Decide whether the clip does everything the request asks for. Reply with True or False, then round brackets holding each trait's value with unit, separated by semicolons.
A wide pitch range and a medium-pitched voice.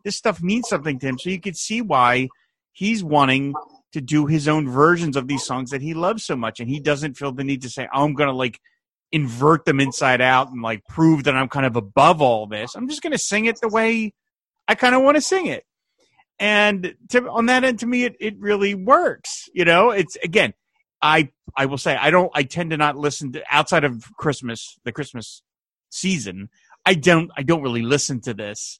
True (7.4 semitones; 155 Hz)